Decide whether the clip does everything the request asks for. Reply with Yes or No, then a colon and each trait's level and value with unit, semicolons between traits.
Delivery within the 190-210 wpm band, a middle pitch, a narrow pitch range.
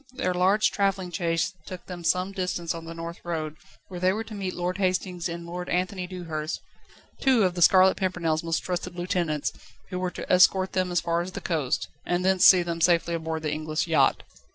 Yes: fast, 205 wpm; medium, 180 Hz; narrow, 1.8 semitones